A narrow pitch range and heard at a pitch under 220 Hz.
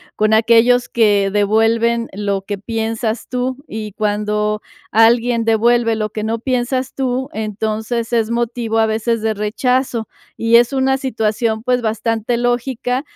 No: narrow, 2.0 semitones; high, 225 Hz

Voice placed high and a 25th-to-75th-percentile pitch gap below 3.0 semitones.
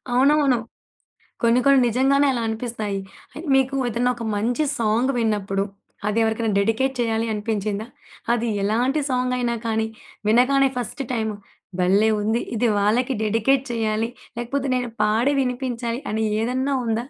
Yes: high, 235 Hz; narrow, 2.5 semitones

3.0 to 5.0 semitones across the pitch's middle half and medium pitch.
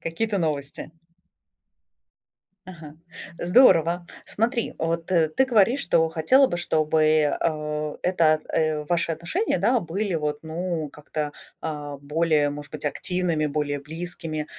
No: narrow, 2.6 semitones; medium, 160 Hz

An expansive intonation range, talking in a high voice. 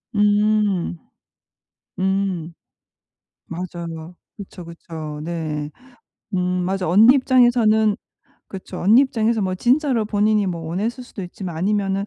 No: average, 3.7 semitones; high, 195 Hz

